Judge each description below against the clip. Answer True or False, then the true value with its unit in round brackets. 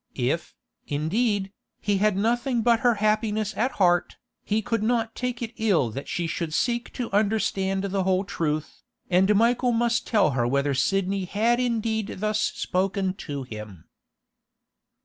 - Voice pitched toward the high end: True (200 Hz)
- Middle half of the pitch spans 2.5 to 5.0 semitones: True (4.4 semitones)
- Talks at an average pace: True (150 wpm)